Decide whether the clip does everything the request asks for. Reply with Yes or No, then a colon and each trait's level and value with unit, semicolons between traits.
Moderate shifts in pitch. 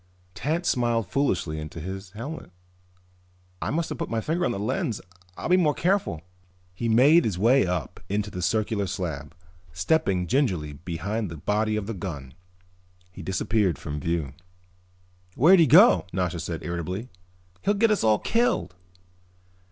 No: wide, 7.7 semitones